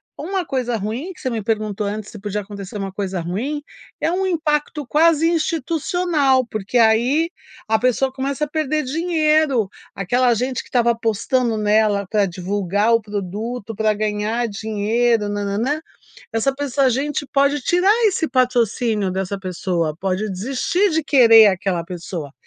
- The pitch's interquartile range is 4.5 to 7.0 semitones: Yes, wide, 5.6 semitones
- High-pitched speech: Yes, high, 230 Hz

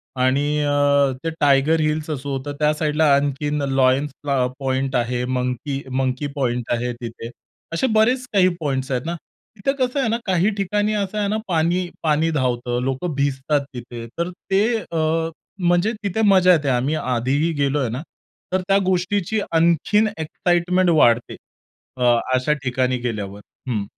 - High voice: No, medium, 145 Hz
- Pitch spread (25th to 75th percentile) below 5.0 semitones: No, average, 5.3 semitones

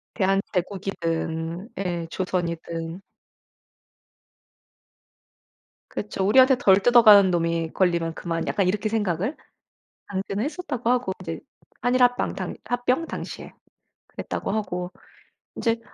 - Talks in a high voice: Yes, high, 195 Hz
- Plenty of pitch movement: No, average, 5.0 semitones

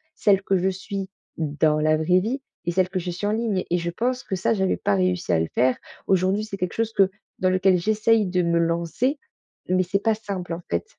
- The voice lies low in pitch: No, medium, 185 Hz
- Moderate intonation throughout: Yes, average, 3.0 semitones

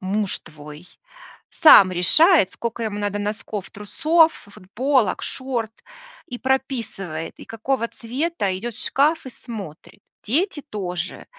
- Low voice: No, high, 225 Hz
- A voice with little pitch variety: No, wide, 5.5 semitones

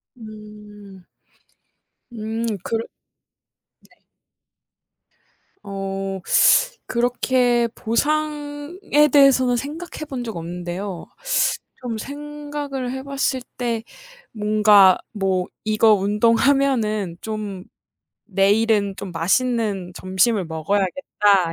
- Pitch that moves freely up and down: No, average, 5.0 semitones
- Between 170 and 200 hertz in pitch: No, high, 220 Hz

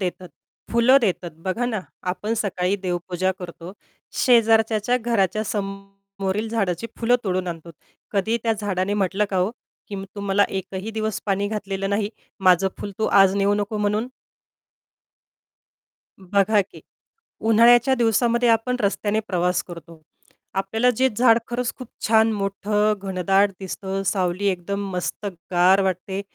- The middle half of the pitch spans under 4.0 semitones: Yes, average, 2.8 semitones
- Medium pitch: No, high, 200 Hz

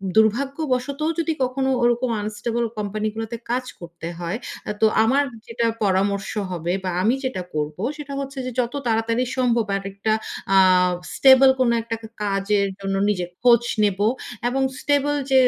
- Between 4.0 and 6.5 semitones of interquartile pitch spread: Yes, average, 4.5 semitones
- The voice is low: No, high, 230 Hz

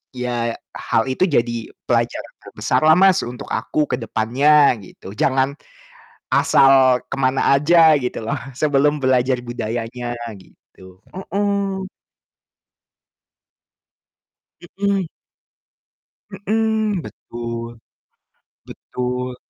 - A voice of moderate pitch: No, low, 130 Hz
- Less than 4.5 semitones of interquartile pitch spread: No, average, 5.3 semitones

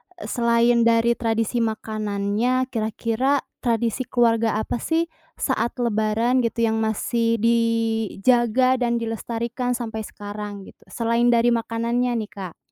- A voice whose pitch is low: No, high, 230 Hz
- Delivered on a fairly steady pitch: Yes, narrow, 1.5 semitones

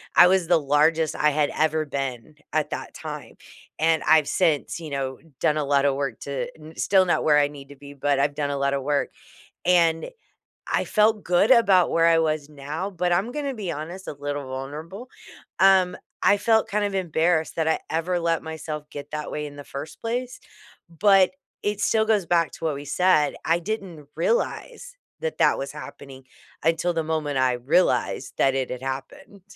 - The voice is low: No, medium, 160 Hz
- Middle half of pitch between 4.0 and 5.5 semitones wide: Yes, average, 4.3 semitones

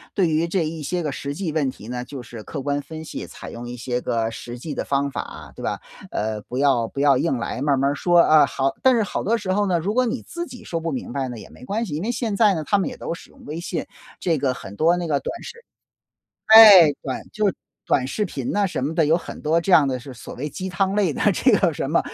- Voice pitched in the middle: Yes, medium, 155 Hz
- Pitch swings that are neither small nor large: No, wide, 6.0 semitones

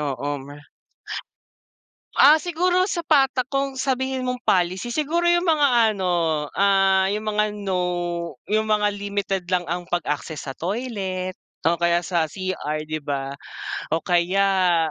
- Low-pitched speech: No, high, 190 Hz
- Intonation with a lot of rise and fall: Yes, wide, 6.6 semitones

